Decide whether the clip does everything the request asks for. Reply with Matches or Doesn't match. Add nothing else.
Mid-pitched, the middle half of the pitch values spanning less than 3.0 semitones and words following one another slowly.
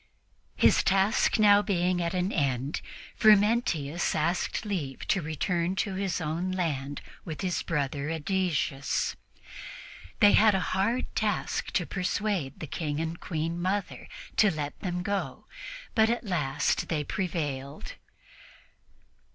Doesn't match